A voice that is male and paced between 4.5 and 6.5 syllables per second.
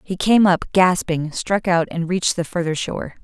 No: female; 5.0 syllables/s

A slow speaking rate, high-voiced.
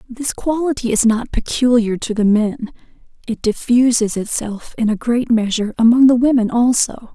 No: average, 160 wpm; high, 235 Hz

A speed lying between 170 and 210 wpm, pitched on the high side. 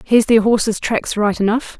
Yes: average, 200 wpm; high, 220 Hz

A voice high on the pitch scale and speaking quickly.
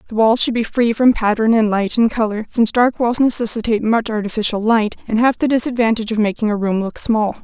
Yes: high, 225 Hz; fast, 225 wpm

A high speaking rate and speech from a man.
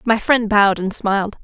No: fast, 210 wpm; female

